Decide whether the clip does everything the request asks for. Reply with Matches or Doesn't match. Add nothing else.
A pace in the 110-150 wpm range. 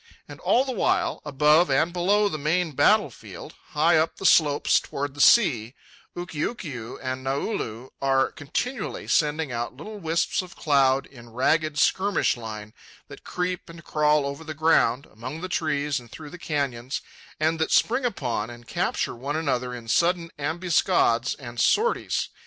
Doesn't match